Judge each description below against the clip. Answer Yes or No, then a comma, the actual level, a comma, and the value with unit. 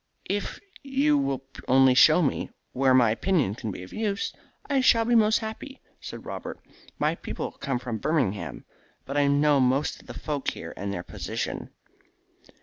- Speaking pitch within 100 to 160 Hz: Yes, medium, 140 Hz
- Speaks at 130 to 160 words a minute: No, average, 175 wpm